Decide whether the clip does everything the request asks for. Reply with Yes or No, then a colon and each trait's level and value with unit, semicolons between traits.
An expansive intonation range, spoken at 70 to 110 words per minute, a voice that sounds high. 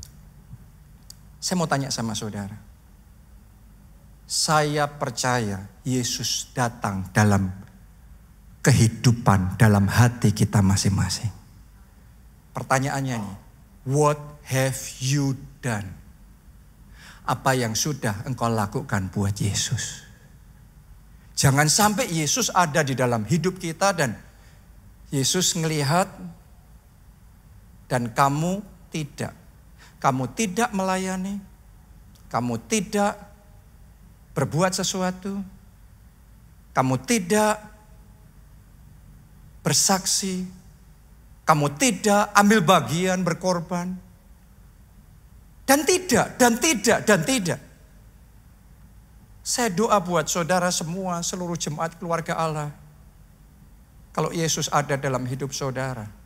No: wide, 8.5 semitones; slow, 85 wpm; medium, 140 Hz